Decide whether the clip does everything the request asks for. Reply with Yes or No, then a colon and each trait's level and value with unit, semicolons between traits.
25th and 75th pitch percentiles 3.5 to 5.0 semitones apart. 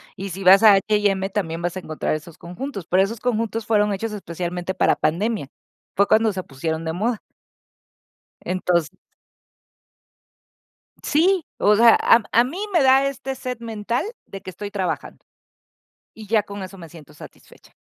Yes: average, 4.2 semitones